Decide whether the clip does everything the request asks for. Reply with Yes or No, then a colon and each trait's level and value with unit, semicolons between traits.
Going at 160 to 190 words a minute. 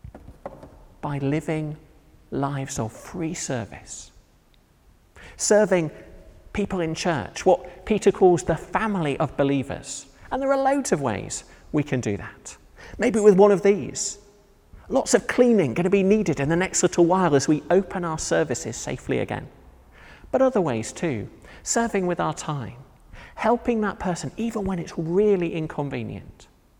No: average, 150 wpm